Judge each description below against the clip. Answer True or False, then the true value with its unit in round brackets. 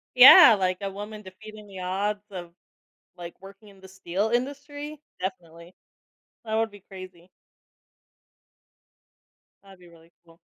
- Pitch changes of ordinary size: True (3.0 semitones)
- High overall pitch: True (195 Hz)